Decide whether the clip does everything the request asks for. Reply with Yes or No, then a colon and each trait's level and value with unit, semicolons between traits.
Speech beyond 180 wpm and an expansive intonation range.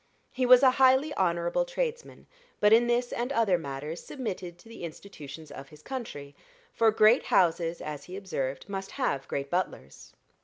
No: average, 170 wpm; wide, 7.4 semitones